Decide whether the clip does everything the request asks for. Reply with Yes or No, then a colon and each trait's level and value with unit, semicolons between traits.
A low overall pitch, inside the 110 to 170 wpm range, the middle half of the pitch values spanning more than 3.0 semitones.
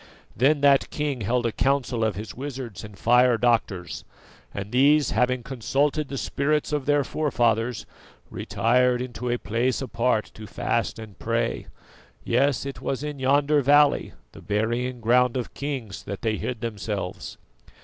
Yes: low, 125 Hz; average, 150 wpm; average, 3.5 semitones